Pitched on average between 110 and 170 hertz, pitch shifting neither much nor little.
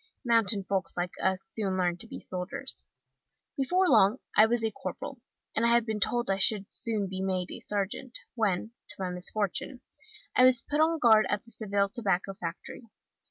No: high, 210 Hz; average, 3.6 semitones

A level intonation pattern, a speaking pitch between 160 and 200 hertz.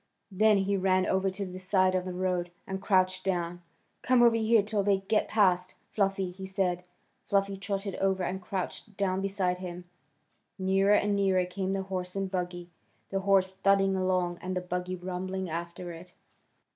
Yes: narrow, 1.3 semitones; high, 190 Hz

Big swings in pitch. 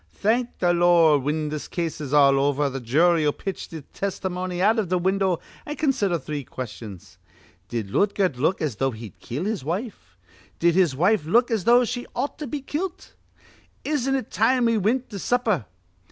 Yes: wide, 7.4 semitones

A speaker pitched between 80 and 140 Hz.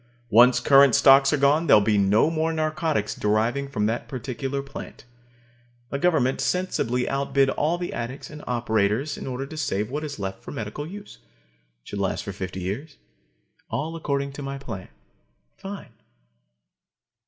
Yes: low, 135 Hz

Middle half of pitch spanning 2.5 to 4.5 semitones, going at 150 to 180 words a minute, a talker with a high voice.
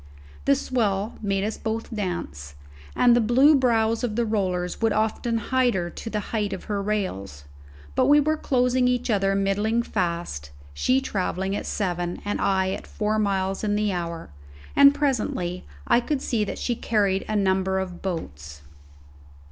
Yes: average, 3.9 semitones; average, 170 wpm; high, 205 Hz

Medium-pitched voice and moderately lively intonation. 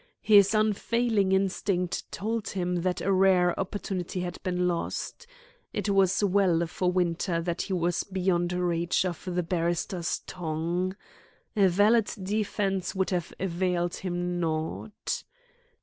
No: medium, 180 Hz; narrow, 1.9 semitones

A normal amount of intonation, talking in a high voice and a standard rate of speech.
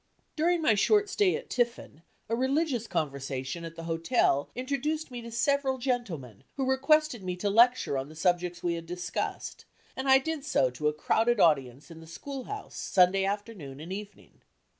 No: wide, 8.3 semitones; high, 210 Hz; average, 180 wpm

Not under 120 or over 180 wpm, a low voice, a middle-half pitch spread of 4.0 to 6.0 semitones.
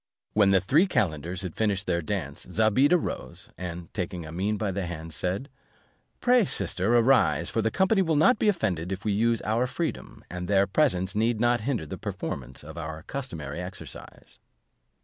Yes: average, 175 wpm; low, 100 Hz; wide, 5.5 semitones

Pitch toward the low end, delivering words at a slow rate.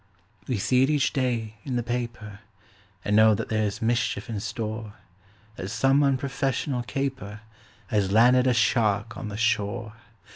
No: low, 115 Hz; average, 150 wpm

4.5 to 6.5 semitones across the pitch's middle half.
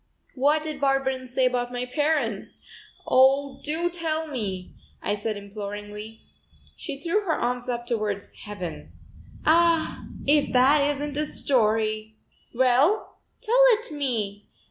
Yes: wide, 5.6 semitones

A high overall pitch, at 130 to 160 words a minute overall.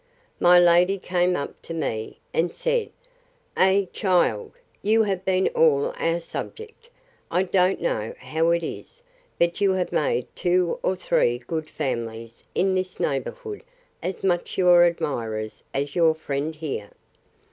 No: medium, 175 Hz; average, 145 wpm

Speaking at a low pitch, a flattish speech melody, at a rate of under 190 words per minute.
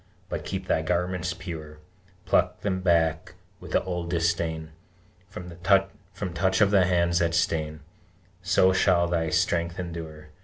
Yes: very low, 85 Hz; narrow, 1.8 semitones; average, 140 wpm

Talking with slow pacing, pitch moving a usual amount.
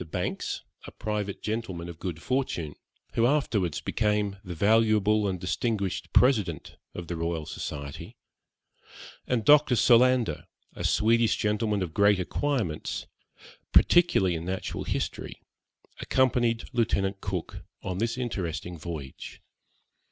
Yes: slow, 115 wpm; average, 4.9 semitones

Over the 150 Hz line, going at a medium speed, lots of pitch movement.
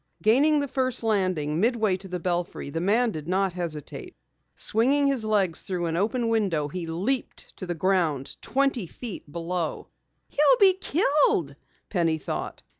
Yes: high, 190 Hz; average, 155 wpm; wide, 6.6 semitones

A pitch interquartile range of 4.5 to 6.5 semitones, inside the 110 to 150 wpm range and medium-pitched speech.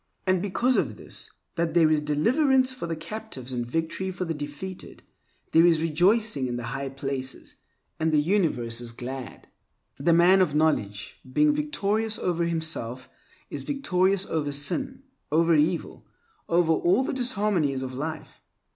Yes: wide, 5.4 semitones; average, 145 wpm; medium, 165 Hz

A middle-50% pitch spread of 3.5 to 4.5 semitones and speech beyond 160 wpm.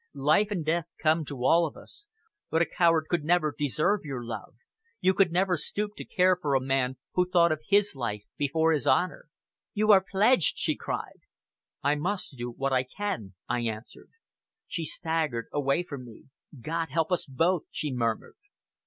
No: average, 5.1 semitones; average, 180 wpm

